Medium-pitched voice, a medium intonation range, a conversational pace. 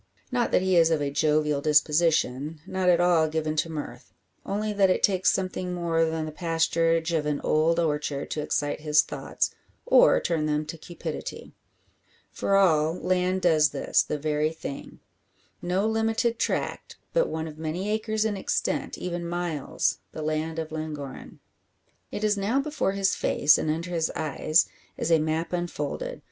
Yes: medium, 165 Hz; average, 3.2 semitones; average, 170 wpm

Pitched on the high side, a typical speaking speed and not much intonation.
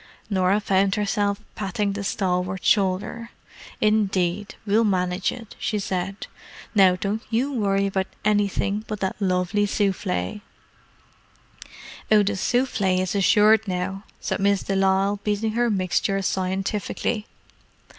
No: high, 200 Hz; slow, 125 wpm; narrow, 1.8 semitones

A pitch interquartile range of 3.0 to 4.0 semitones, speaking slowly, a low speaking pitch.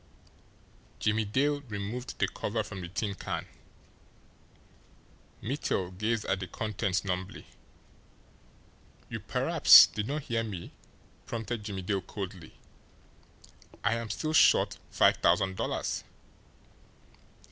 Yes: average, 3.4 semitones; slow, 110 wpm; low, 105 Hz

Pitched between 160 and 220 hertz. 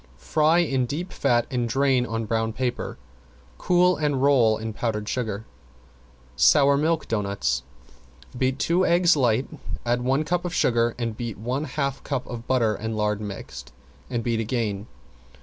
No: low, 120 Hz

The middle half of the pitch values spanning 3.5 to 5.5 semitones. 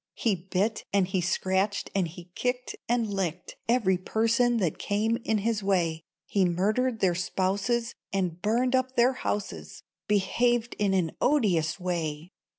Yes: average, 4.3 semitones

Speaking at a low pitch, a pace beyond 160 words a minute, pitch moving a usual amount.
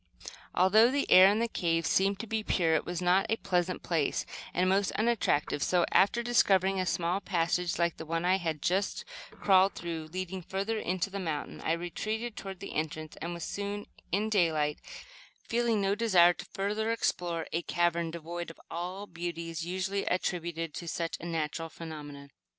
No: medium, 180 Hz; average, 180 wpm; average, 3.0 semitones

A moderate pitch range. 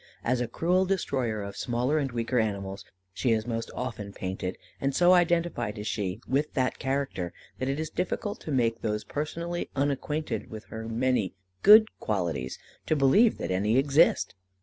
No: wide, 6.1 semitones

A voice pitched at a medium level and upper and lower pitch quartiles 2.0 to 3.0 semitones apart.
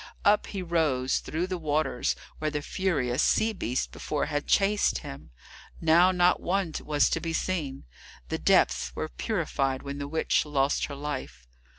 No: medium, 150 Hz; average, 4.5 semitones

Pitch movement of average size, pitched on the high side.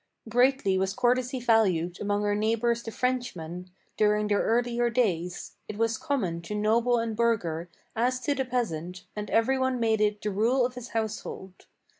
Yes: average, 3.3 semitones; high, 225 Hz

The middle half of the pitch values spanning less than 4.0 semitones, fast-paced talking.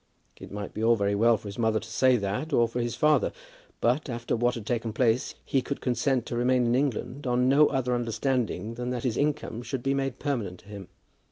Yes: average, 2.8 semitones; fast, 230 wpm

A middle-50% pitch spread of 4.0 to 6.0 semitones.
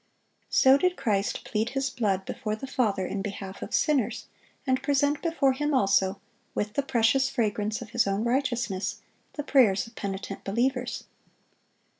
Yes: average, 5.0 semitones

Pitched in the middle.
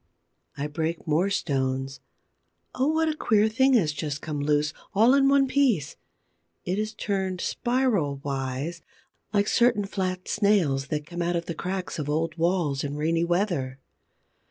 Yes: medium, 175 Hz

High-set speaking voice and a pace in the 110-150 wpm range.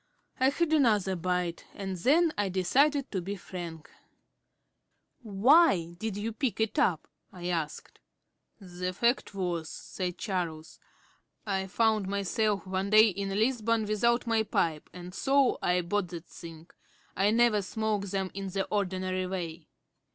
Yes: high, 195 Hz; average, 145 wpm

